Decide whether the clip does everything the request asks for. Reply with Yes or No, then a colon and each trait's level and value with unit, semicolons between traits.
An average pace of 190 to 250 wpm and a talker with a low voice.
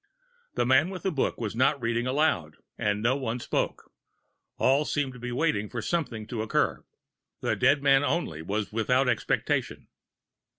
No: average, 165 wpm; low, 125 Hz